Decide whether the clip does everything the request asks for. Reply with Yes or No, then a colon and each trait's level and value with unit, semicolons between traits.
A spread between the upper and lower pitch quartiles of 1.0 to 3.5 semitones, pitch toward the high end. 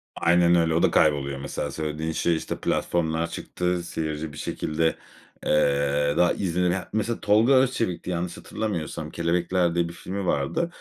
No: narrow, 2.6 semitones; very low, 85 Hz